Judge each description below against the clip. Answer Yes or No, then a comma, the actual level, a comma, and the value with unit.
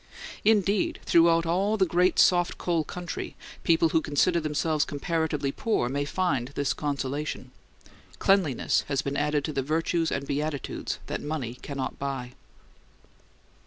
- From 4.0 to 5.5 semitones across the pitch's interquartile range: No, average, 3.6 semitones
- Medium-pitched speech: Yes, medium, 155 Hz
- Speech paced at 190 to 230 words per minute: No, average, 140 wpm